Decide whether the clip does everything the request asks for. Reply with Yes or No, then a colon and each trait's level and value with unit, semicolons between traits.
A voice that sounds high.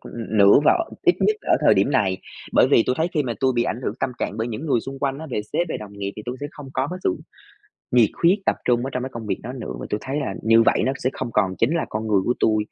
No: low, 120 Hz